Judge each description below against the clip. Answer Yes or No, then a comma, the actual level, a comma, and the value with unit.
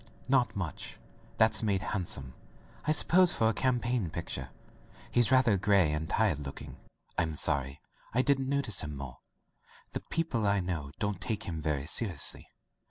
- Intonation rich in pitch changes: Yes, wide, 7.9 semitones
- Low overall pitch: Yes, low, 100 Hz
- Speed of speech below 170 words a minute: Yes, average, 160 wpm